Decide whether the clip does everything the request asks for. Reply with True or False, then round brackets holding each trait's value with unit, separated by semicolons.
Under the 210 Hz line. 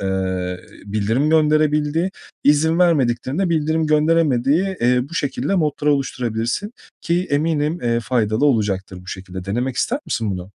True (140 Hz)